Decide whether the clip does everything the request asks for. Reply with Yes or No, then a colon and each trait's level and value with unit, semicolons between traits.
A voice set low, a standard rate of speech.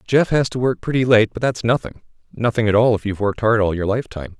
No: low, 115 Hz; fast, 245 wpm